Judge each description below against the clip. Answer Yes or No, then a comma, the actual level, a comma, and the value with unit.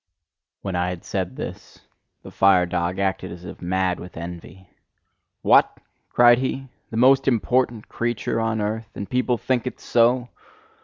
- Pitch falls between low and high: No, low, 110 Hz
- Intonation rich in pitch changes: No, average, 5.0 semitones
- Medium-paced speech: Yes, average, 155 wpm